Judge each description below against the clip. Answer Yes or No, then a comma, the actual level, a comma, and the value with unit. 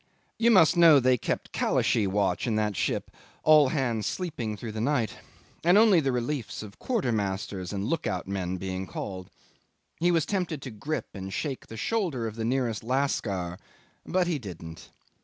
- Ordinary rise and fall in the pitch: No, wide, 7.6 semitones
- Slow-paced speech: No, average, 175 wpm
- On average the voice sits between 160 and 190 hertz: No, low, 120 Hz